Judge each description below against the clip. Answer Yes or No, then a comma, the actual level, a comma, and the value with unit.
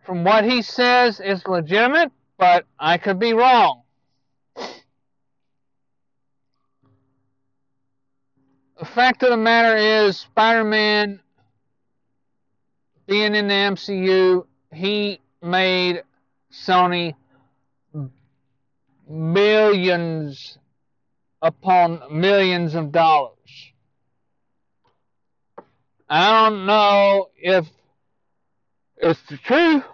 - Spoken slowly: Yes, slow, 75 wpm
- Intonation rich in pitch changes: Yes, wide, 7.4 semitones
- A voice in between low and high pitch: Yes, medium, 180 Hz